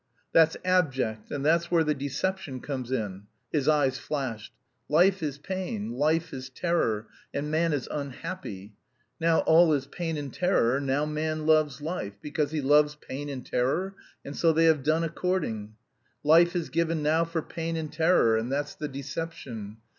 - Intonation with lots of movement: No, average, 3.8 semitones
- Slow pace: No, average, 170 wpm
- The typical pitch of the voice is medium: Yes, medium, 150 Hz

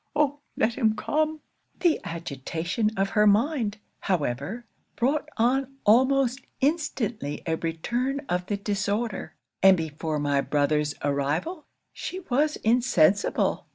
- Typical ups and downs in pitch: No, wide, 8.7 semitones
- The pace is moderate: No, slow, 120 wpm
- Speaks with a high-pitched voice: Yes, high, 210 Hz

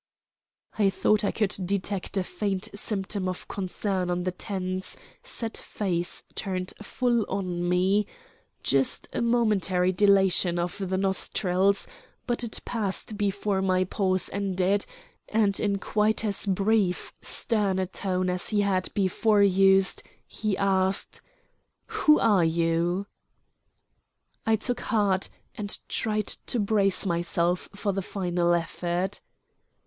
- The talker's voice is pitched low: No, high, 195 Hz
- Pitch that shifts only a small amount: Yes, narrow, 2.1 semitones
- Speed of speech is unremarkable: No, slow, 125 wpm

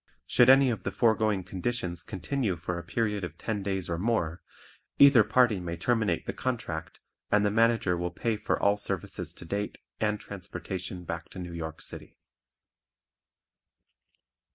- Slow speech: No, average, 155 wpm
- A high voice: No, low, 100 Hz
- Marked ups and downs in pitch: No, average, 4.4 semitones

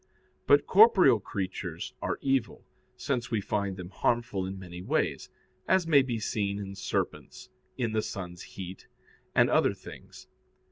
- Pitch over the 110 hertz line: No, low, 105 Hz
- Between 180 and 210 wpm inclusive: No, average, 145 wpm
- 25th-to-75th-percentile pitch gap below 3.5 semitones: No, average, 5.1 semitones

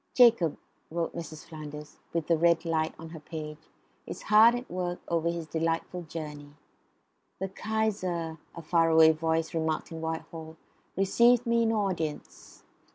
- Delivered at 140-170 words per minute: Yes, average, 150 wpm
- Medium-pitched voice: Yes, medium, 165 Hz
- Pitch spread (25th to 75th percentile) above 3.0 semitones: No, narrow, 2.6 semitones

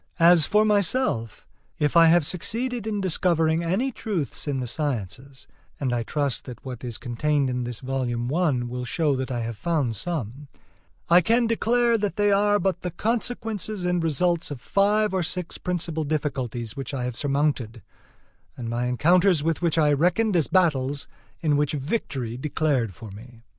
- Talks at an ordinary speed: Yes, average, 175 wpm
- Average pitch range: No, wide, 6.3 semitones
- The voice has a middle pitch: Yes, medium, 150 Hz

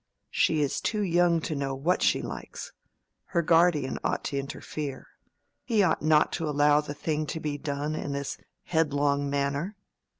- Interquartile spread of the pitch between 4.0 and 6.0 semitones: No, narrow, 2.6 semitones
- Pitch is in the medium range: Yes, medium, 150 Hz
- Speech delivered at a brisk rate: No, average, 165 wpm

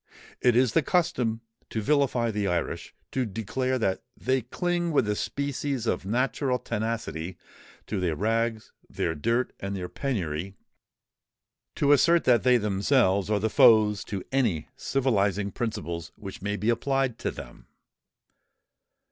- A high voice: No, low, 115 Hz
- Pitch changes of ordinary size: Yes, average, 4.7 semitones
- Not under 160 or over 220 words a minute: No, slow, 135 wpm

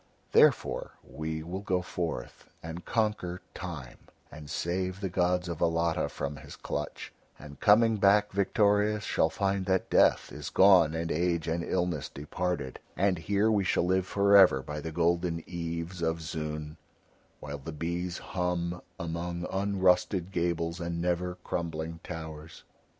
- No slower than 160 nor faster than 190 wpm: No, average, 145 wpm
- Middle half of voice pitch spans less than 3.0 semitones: Yes, narrow, 2.4 semitones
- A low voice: Yes, very low, 85 Hz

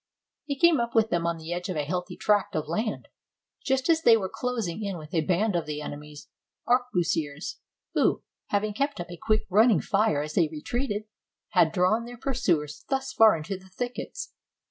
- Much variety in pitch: Yes, wide, 6.1 semitones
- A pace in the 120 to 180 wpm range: No, average, 195 wpm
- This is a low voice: No, high, 195 Hz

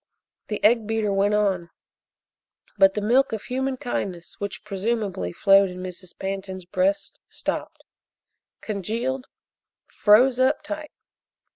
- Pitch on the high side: Yes, high, 210 Hz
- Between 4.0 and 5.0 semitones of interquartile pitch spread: Yes, average, 4.5 semitones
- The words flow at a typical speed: No, slow, 120 wpm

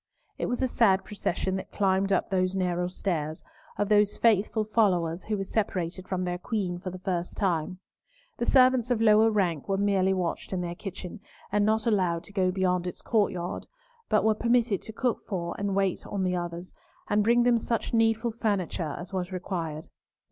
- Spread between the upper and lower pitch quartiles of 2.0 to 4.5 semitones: Yes, average, 3.1 semitones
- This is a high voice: Yes, high, 195 Hz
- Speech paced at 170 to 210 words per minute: Yes, average, 190 wpm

